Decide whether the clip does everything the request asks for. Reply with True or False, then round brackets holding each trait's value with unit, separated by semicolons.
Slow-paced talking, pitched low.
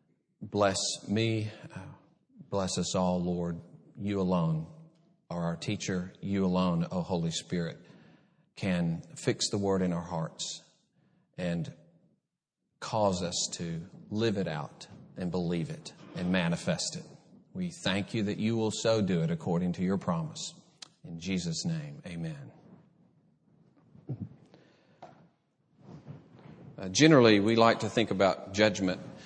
True (125 wpm; 110 Hz)